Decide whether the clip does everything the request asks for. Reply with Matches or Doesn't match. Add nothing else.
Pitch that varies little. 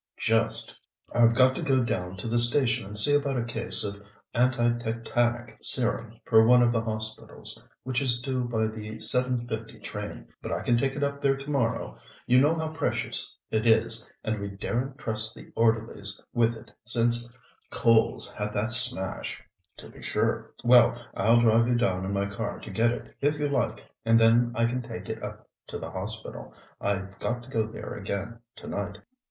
Matches